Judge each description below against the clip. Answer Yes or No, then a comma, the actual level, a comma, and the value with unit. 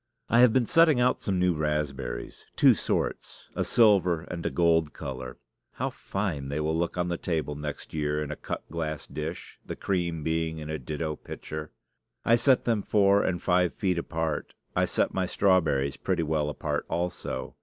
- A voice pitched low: Yes, very low, 80 Hz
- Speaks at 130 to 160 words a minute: No, average, 185 wpm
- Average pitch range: Yes, average, 3.6 semitones